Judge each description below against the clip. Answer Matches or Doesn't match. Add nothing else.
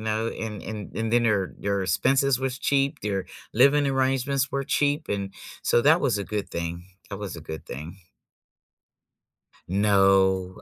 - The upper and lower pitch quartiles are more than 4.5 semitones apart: Matches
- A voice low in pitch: Matches